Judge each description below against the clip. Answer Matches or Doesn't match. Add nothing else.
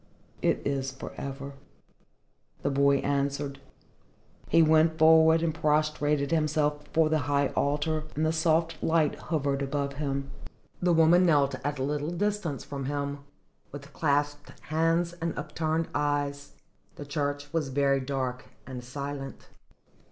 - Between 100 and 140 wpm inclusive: Matches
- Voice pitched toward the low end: Doesn't match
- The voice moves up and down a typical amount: Doesn't match